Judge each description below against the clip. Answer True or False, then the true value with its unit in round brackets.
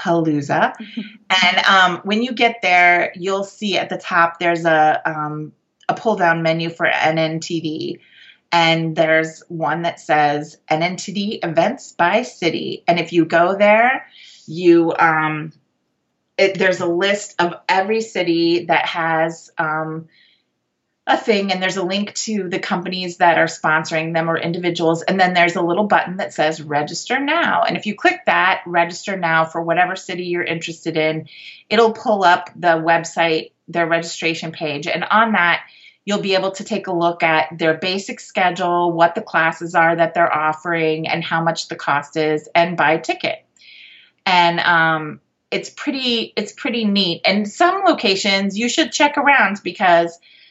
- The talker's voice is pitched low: False (170 Hz)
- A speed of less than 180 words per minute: True (165 wpm)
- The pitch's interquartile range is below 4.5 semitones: True (3.2 semitones)